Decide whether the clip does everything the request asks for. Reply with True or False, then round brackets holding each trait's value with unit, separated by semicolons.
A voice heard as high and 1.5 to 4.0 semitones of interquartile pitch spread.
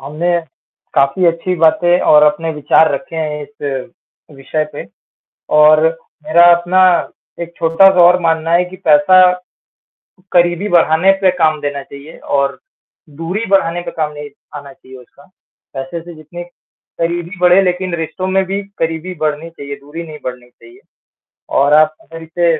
False (165 Hz; 2.8 semitones)